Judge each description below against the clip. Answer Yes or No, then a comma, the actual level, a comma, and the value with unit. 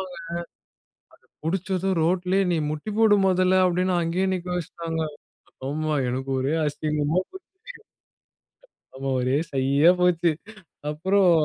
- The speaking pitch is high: No, medium, 170 Hz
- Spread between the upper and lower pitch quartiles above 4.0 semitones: No, average, 3.6 semitones